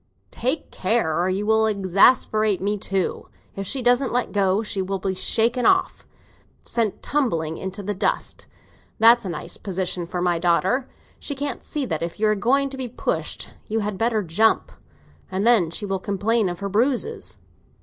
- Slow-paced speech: No, average, 175 wpm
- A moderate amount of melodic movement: Yes, average, 4.0 semitones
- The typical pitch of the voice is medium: No, high, 205 Hz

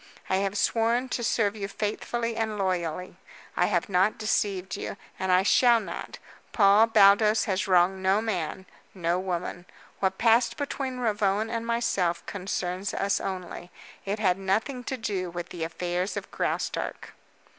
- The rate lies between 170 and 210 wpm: No, average, 155 wpm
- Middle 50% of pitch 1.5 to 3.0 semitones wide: No, average, 3.4 semitones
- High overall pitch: Yes, high, 195 Hz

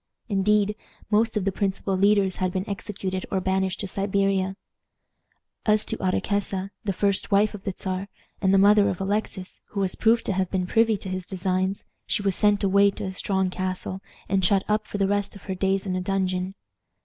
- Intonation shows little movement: Yes, narrow, 1.4 semitones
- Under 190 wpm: No, average, 200 wpm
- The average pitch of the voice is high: Yes, high, 195 Hz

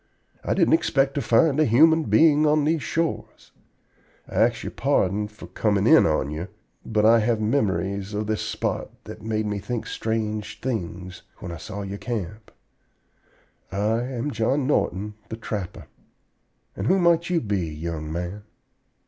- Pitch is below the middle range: Yes, low, 110 Hz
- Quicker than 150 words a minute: Yes, average, 160 wpm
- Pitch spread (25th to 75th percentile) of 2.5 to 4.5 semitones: No, wide, 5.6 semitones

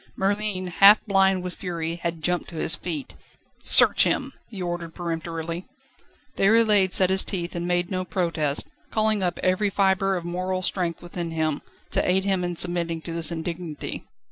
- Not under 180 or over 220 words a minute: No, average, 170 wpm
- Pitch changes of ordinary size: No, narrow, 2.3 semitones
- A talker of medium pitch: Yes, medium, 180 Hz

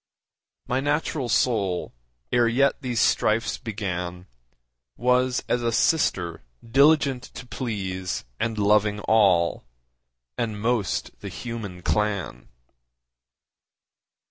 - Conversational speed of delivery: No, slow, 95 wpm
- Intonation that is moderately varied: Yes, average, 4.3 semitones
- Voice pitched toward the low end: Yes, low, 110 Hz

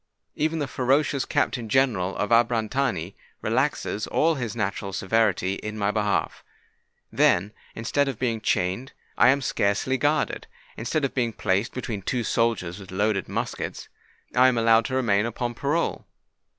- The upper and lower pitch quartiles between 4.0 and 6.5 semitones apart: Yes, average, 4.3 semitones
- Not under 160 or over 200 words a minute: No, average, 150 wpm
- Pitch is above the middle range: No, low, 115 Hz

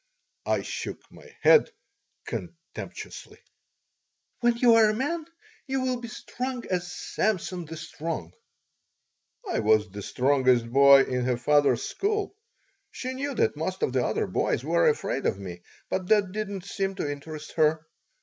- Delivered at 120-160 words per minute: Yes, average, 155 wpm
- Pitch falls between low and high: Yes, medium, 180 Hz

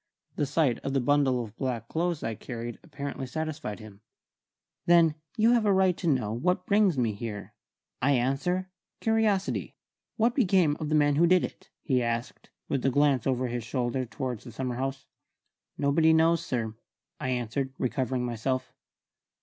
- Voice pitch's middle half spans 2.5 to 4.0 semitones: No, average, 5.3 semitones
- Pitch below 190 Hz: Yes, low, 135 Hz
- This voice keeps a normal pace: Yes, average, 165 wpm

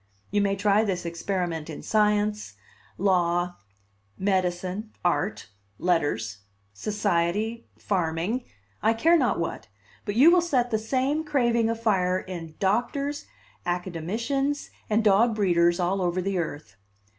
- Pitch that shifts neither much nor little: Yes, average, 4.4 semitones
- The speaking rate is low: Yes, slow, 120 wpm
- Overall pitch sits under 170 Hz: No, high, 200 Hz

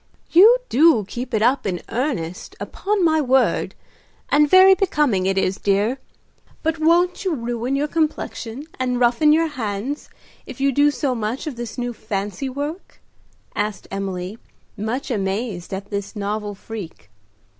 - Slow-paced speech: No, average, 150 wpm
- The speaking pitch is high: Yes, high, 245 Hz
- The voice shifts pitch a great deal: Yes, wide, 6.4 semitones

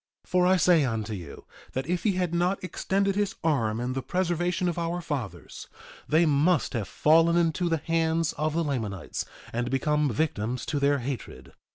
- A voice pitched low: No, medium, 160 Hz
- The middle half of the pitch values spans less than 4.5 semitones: No, average, 5.0 semitones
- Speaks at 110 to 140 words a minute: No, average, 185 wpm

